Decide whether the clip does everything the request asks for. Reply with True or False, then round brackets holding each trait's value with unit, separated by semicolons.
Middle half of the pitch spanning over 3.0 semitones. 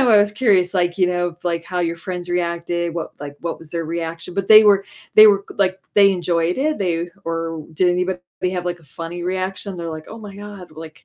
False (2.6 semitones)